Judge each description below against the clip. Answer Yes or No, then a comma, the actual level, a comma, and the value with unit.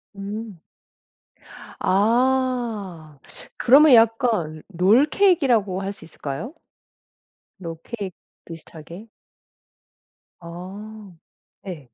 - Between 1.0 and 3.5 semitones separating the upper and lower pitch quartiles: No, wide, 5.4 semitones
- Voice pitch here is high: Yes, high, 205 Hz